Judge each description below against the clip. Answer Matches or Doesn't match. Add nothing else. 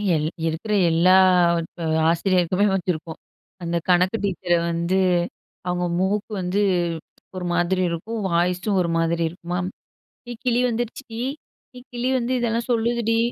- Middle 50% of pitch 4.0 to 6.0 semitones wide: Matches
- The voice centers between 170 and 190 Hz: Matches